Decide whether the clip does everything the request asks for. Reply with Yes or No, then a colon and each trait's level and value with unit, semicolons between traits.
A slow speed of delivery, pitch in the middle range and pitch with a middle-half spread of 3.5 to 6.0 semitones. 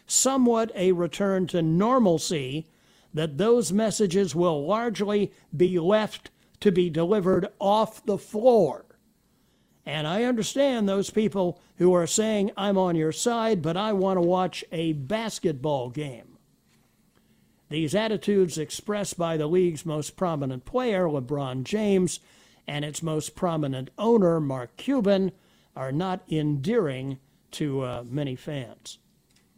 Yes: slow, 130 wpm; medium, 180 Hz; average, 5.2 semitones